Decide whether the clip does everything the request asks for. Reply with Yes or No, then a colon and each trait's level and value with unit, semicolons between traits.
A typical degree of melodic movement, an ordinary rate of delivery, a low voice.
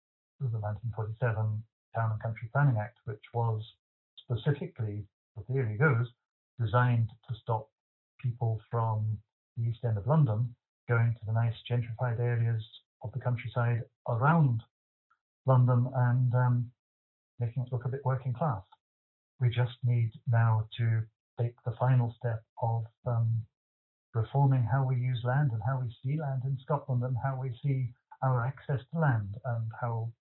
No: narrow, 2.3 semitones; average, 150 wpm; low, 120 Hz